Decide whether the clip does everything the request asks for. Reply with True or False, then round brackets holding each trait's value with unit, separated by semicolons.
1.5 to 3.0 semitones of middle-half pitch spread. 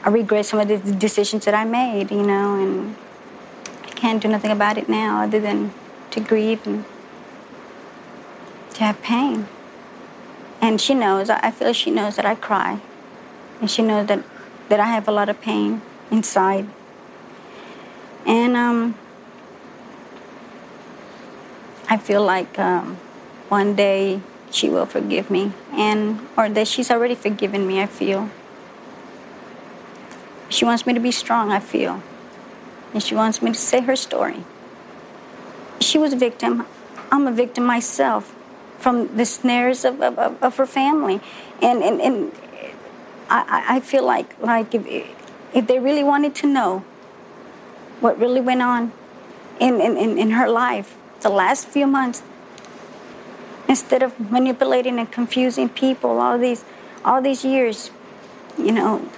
False (3.5 semitones)